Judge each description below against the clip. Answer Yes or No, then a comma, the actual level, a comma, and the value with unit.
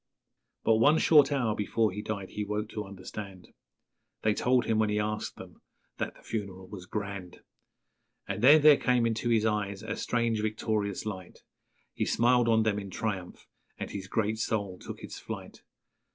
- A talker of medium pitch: No, low, 105 Hz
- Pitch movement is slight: Yes, narrow, 2.2 semitones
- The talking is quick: No, average, 180 wpm